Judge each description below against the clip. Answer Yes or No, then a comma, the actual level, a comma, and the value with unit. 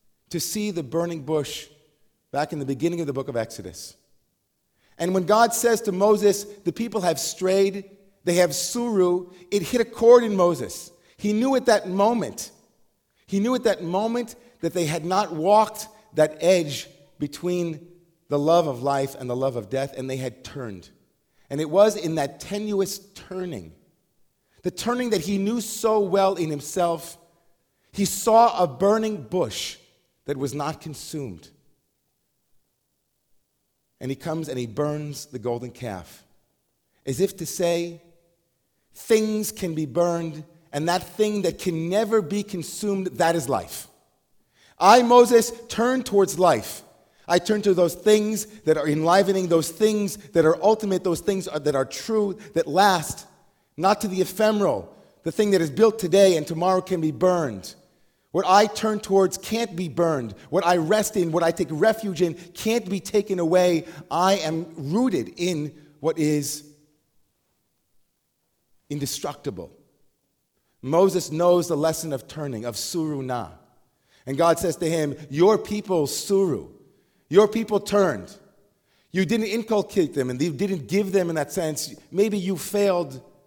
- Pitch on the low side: No, medium, 175 Hz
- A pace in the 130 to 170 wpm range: Yes, average, 160 wpm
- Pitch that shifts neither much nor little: Yes, average, 4.8 semitones